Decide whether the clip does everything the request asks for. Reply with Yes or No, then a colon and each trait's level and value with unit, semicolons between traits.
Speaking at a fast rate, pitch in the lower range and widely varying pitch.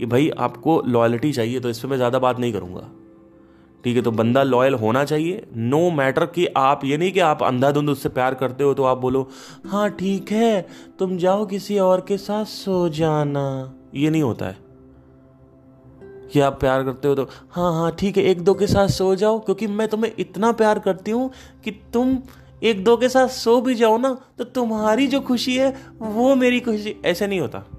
No: fast, 205 wpm; medium, 160 Hz; wide, 8.4 semitones